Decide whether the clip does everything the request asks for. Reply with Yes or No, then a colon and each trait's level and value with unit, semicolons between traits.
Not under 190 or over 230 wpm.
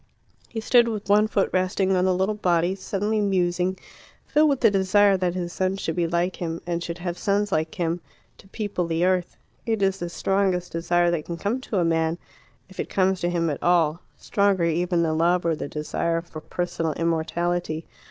Yes: average, 200 wpm